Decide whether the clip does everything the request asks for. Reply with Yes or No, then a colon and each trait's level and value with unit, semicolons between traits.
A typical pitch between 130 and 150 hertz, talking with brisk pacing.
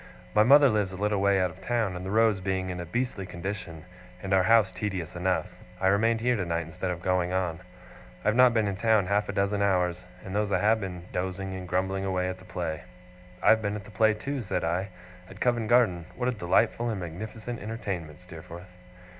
No: very low, 95 Hz; fast, 220 wpm